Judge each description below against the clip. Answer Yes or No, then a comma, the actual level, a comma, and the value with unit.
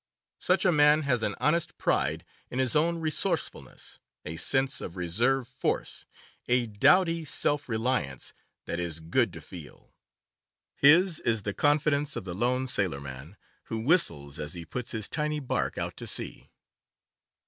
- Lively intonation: Yes, wide, 8.2 semitones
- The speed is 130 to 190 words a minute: Yes, average, 150 wpm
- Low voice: Yes, low, 125 Hz